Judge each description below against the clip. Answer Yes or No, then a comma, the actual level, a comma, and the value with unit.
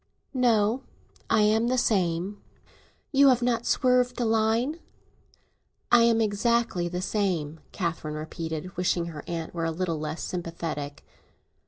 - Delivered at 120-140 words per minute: Yes, slow, 135 wpm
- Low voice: No, high, 195 Hz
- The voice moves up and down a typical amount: No, wide, 5.8 semitones